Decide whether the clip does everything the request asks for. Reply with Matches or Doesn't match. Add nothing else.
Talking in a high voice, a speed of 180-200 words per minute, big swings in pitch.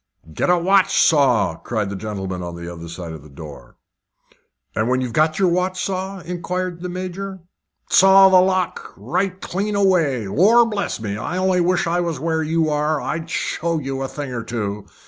Doesn't match